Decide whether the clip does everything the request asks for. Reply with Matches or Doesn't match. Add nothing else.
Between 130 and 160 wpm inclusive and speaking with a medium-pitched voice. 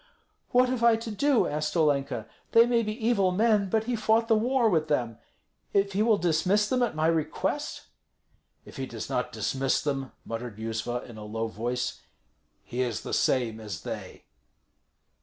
Doesn't match